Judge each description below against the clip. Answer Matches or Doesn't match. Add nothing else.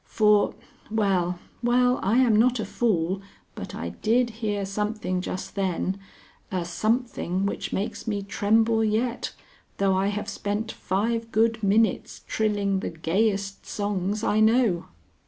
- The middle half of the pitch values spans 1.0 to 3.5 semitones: Matches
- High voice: Matches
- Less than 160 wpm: Matches